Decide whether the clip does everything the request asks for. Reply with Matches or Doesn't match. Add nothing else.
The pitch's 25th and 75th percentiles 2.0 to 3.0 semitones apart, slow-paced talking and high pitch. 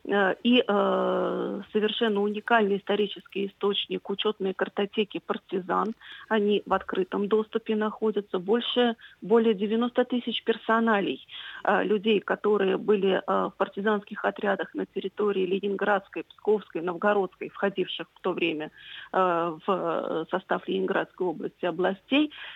Matches